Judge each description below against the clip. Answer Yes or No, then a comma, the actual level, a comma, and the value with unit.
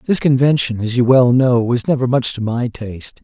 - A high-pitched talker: No, low, 125 Hz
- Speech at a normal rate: No, fast, 220 wpm